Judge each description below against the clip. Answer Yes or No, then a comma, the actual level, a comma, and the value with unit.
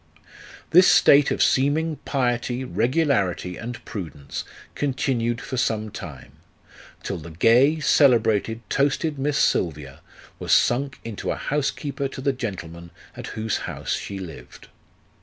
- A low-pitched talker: Yes, low, 120 Hz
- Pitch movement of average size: No, wide, 5.8 semitones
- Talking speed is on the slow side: Yes, slow, 130 wpm